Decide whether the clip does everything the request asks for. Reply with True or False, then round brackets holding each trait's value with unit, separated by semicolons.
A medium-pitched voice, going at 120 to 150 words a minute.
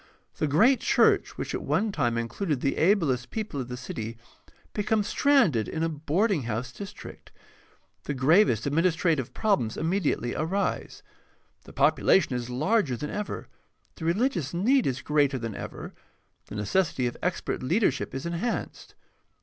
True (155 Hz; 145 wpm)